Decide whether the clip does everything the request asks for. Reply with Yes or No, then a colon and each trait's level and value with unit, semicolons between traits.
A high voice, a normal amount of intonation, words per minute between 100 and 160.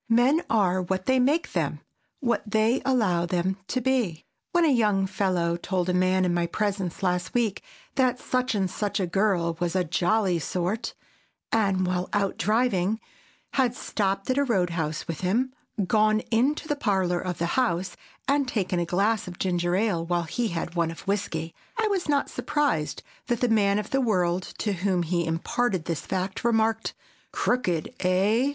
No: high, 195 Hz; average, 4.8 semitones; average, 175 wpm